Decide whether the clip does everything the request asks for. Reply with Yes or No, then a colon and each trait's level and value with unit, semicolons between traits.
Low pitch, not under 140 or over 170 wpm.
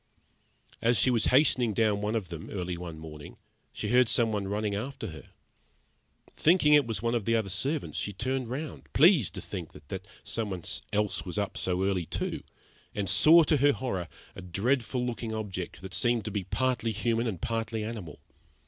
No: low, 110 Hz; average, 185 wpm